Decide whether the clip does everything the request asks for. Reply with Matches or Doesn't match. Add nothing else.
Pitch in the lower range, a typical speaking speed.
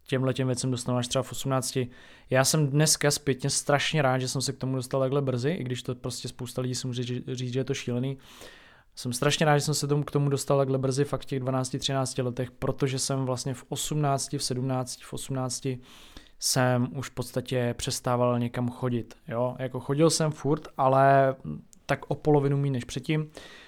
Doesn't match